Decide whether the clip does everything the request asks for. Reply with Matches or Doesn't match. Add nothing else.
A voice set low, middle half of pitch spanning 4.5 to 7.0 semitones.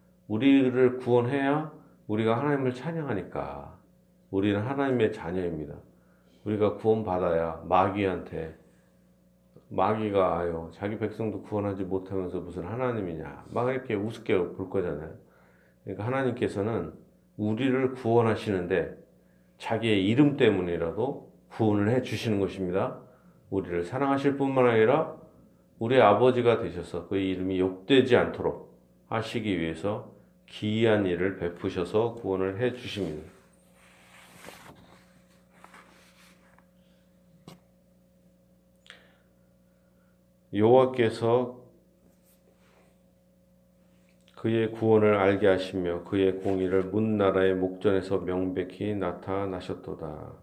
Matches